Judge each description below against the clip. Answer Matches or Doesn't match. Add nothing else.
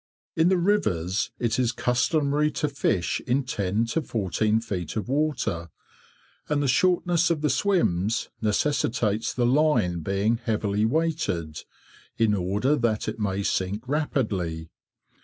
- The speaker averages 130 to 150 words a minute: Matches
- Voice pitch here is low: Matches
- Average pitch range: Doesn't match